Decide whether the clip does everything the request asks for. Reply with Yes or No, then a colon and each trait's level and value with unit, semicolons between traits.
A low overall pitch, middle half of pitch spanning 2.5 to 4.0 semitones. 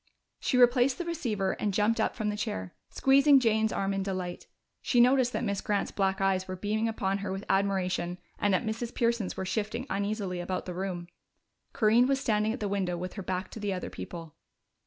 No: high, 205 Hz; average, 3.3 semitones